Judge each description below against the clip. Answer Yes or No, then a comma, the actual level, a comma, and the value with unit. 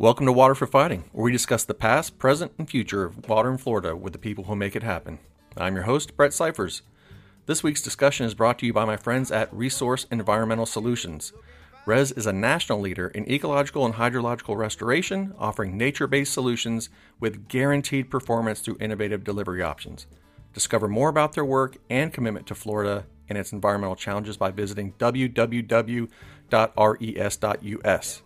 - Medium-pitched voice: No, low, 115 Hz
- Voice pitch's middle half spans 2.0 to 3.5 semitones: No, average, 4.0 semitones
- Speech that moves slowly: No, average, 170 wpm